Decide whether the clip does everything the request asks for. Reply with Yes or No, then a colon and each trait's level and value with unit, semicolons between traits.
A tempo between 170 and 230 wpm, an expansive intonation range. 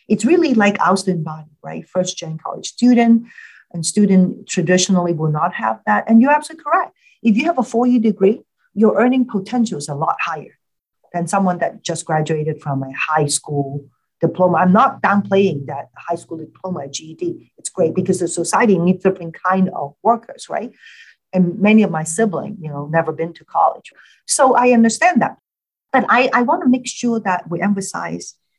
Yes: average, 185 wpm; wide, 5.7 semitones